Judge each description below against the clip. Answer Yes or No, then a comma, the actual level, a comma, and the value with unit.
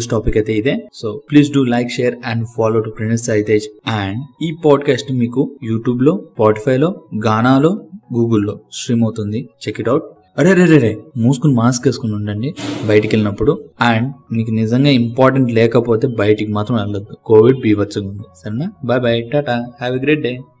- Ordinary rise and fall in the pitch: Yes, average, 4.0 semitones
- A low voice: Yes, low, 120 Hz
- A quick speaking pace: Yes, fast, 165 wpm